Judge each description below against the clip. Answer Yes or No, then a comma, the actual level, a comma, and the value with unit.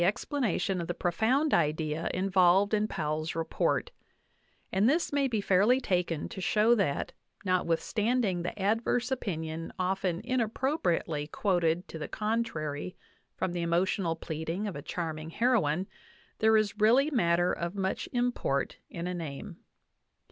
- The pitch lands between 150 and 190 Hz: Yes, medium, 185 Hz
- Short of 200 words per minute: Yes, average, 140 wpm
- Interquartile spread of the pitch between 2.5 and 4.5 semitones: No, average, 4.9 semitones